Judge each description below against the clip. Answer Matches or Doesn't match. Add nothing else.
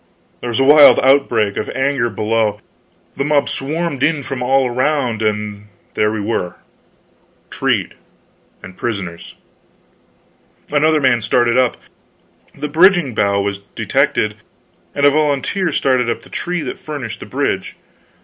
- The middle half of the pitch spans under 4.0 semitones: Doesn't match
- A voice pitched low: Matches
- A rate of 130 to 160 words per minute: Matches